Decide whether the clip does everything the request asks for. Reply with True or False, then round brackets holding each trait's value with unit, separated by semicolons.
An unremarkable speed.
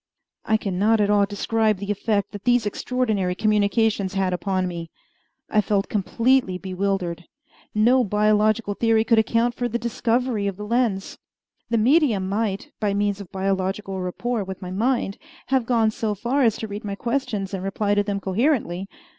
True (170 wpm)